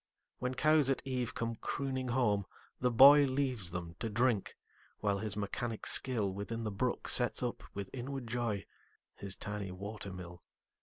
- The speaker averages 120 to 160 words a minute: Yes, average, 145 wpm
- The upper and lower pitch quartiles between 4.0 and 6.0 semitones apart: Yes, average, 4.3 semitones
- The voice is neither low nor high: No, low, 115 Hz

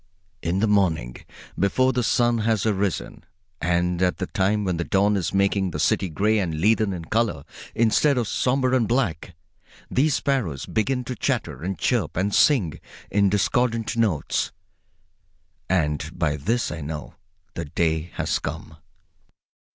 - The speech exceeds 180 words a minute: No, average, 150 wpm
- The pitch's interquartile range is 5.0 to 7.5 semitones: Yes, average, 5.3 semitones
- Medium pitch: No, low, 100 Hz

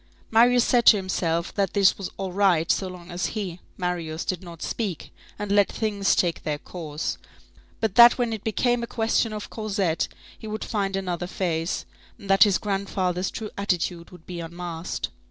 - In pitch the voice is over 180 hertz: Yes, high, 190 Hz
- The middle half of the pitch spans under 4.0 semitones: Yes, average, 3.4 semitones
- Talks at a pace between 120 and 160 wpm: No, average, 180 wpm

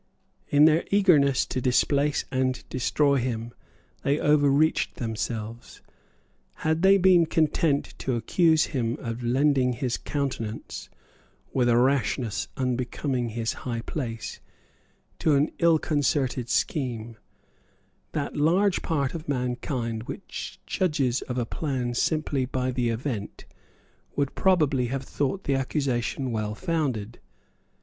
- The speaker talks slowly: Yes, slow, 120 wpm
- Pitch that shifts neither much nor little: Yes, average, 3.8 semitones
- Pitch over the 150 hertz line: No, low, 130 Hz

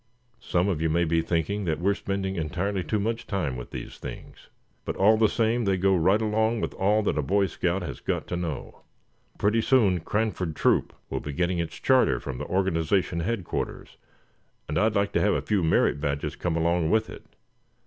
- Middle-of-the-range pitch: No, very low, 95 Hz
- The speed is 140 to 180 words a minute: No, average, 200 wpm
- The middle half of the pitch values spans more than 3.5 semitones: Yes, average, 4.2 semitones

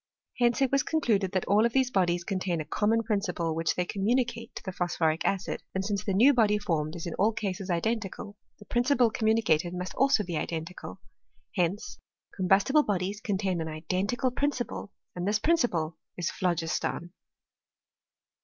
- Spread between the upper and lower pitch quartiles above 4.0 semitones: Yes, average, 4.6 semitones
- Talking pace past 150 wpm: Yes, average, 175 wpm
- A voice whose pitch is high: Yes, high, 195 Hz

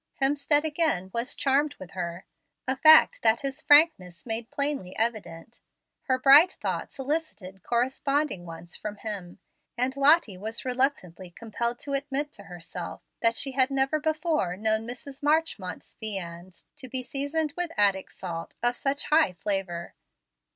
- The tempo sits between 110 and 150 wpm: Yes, average, 145 wpm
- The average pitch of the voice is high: Yes, high, 245 Hz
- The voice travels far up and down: Yes, wide, 7.1 semitones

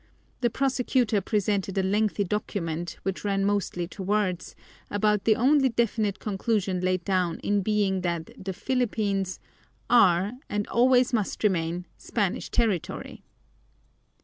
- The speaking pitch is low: No, high, 205 Hz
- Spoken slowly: Yes, slow, 130 wpm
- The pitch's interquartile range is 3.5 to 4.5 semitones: No, average, 3.1 semitones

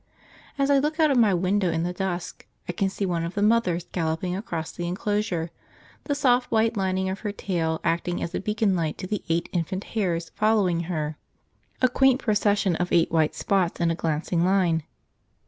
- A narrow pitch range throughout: No, average, 3.8 semitones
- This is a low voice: No, medium, 185 Hz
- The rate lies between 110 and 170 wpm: No, average, 200 wpm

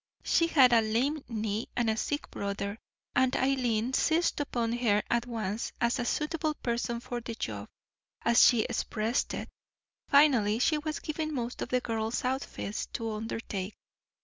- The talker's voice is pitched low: No, high, 235 Hz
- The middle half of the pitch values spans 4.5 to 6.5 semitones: No, average, 3.5 semitones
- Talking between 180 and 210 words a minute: No, average, 160 wpm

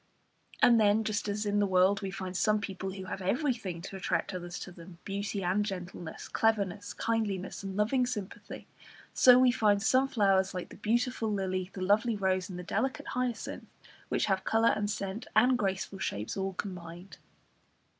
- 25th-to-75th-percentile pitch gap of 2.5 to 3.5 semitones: Yes, average, 2.8 semitones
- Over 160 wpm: Yes, average, 175 wpm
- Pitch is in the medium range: No, high, 200 Hz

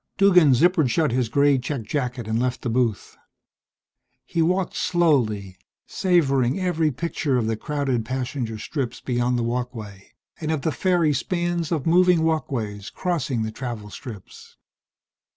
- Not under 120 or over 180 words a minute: Yes, average, 145 wpm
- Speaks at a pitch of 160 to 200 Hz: No, low, 135 Hz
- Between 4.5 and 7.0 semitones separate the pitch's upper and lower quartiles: Yes, wide, 5.6 semitones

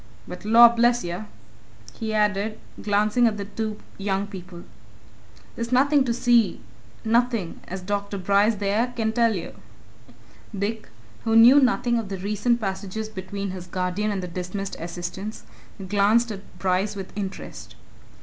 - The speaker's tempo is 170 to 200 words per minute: No, average, 145 wpm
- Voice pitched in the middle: No, high, 205 Hz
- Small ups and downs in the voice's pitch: No, average, 3.1 semitones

